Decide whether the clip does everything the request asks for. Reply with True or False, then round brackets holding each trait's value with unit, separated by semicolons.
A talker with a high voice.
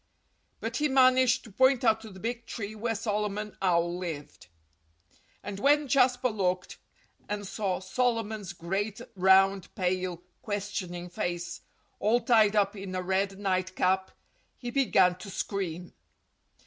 True (200 Hz)